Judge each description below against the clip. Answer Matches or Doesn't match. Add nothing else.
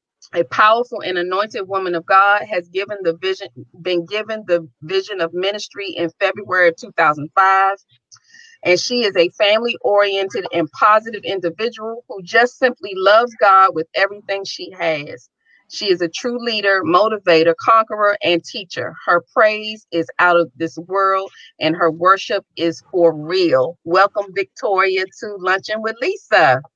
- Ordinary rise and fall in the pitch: Matches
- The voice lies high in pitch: Matches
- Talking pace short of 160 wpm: Matches